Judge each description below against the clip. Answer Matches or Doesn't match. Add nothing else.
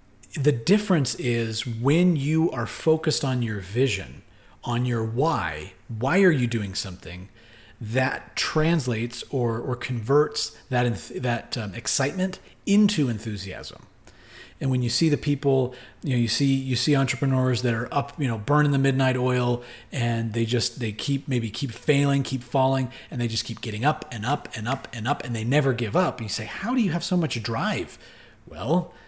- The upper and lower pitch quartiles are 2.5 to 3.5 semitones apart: Doesn't match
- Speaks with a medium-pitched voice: Doesn't match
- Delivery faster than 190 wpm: Doesn't match